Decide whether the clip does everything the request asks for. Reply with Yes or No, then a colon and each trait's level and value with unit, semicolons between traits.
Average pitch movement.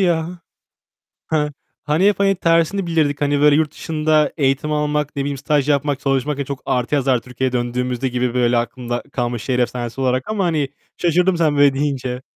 Yes: average, 3.4 semitones